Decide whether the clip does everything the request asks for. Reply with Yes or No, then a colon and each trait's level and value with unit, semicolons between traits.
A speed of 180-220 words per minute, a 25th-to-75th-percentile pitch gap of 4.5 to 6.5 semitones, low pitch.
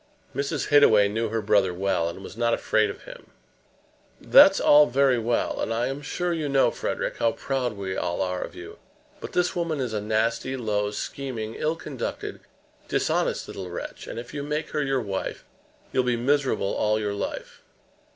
Yes: average, 185 wpm; average, 5.0 semitones; low, 120 Hz